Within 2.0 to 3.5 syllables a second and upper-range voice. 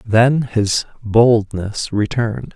No: 3.1 syllables/s; low, 110 Hz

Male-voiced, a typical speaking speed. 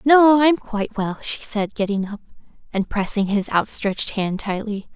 No: female; average, 170 wpm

